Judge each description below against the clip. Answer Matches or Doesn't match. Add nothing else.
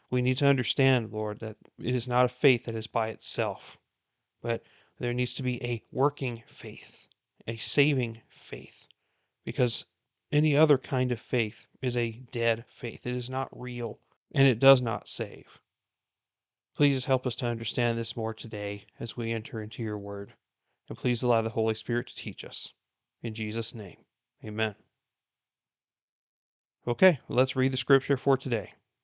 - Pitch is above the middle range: Doesn't match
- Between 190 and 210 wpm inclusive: Doesn't match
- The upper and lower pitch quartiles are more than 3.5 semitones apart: Doesn't match